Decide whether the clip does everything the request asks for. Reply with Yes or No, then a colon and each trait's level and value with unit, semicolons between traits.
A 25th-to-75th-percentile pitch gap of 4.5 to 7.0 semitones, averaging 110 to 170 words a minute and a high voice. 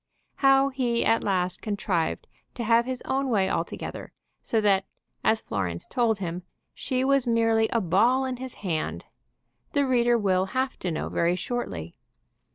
Yes: wide, 5.4 semitones; average, 160 wpm; high, 225 Hz